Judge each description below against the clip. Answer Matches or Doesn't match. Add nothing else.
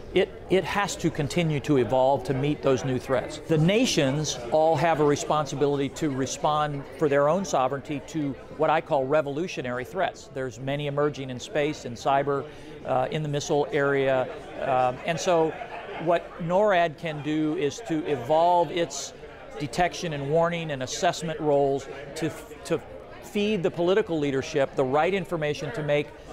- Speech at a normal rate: Matches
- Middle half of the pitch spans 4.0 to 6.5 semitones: Doesn't match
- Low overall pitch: Doesn't match